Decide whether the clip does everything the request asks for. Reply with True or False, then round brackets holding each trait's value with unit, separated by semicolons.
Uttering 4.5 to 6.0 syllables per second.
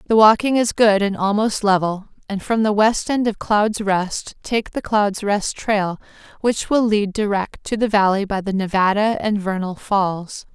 False (4.3 syllables/s)